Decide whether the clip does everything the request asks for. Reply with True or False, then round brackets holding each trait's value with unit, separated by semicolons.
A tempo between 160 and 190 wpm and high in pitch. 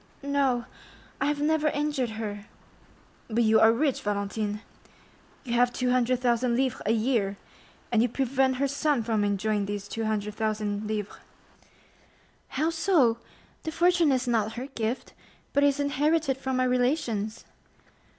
False (135 wpm; 245 Hz)